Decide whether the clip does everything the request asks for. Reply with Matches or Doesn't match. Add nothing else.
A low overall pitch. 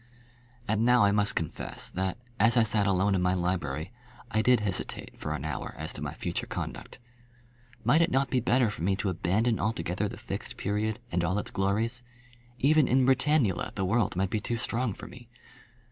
Matches